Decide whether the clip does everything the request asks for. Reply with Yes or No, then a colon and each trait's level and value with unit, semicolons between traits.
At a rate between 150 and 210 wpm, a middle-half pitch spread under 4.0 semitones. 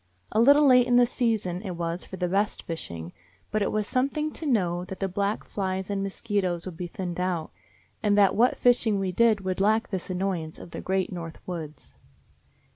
Yes: average, 200 wpm; average, 3.6 semitones